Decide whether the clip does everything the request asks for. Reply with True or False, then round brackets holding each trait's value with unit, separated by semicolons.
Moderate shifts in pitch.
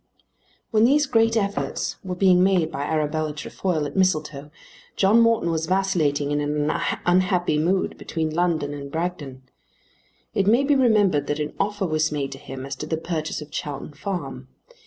True (4.7 semitones)